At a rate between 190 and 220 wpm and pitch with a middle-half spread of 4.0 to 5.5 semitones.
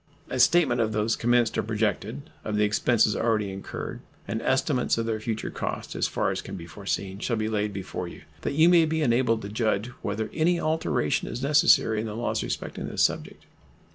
No: average, 200 wpm; average, 3.5 semitones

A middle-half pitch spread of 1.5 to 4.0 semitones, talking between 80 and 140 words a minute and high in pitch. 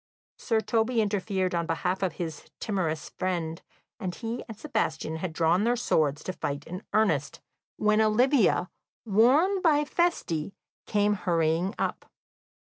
No: average, 5.3 semitones; slow, 135 wpm; high, 195 Hz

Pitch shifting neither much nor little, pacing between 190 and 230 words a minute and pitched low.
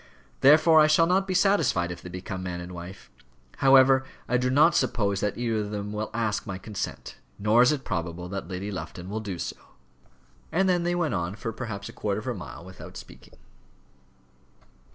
No: wide, 6.4 semitones; average, 195 wpm; low, 105 Hz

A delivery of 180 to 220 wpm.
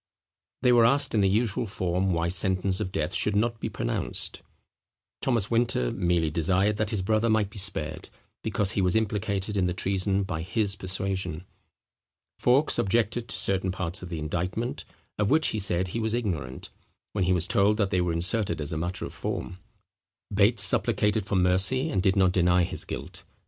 Yes: average, 185 wpm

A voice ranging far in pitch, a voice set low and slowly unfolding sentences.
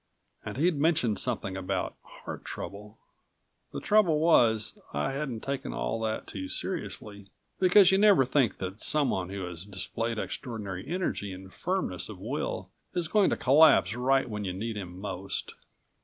No: wide, 7.6 semitones; low, 110 Hz; average, 155 wpm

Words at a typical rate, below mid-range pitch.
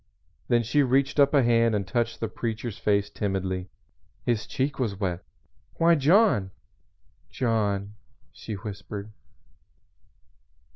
No: slow, 115 wpm; low, 115 Hz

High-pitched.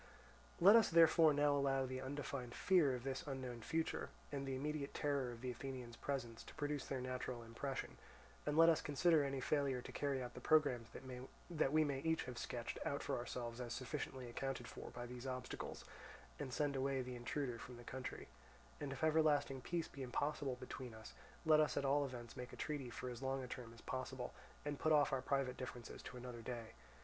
No: low, 135 Hz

